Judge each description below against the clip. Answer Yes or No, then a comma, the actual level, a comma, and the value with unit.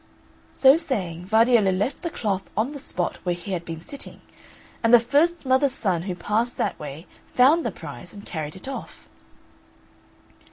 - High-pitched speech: Yes, high, 215 Hz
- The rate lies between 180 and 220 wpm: No, average, 170 wpm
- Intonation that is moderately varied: No, wide, 6.8 semitones